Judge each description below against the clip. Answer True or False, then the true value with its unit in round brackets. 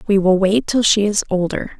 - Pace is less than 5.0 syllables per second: False (5.1 syllables/s)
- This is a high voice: True (200 Hz)